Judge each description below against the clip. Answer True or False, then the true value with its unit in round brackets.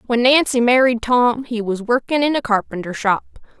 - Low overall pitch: False (240 Hz)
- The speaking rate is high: False (185 wpm)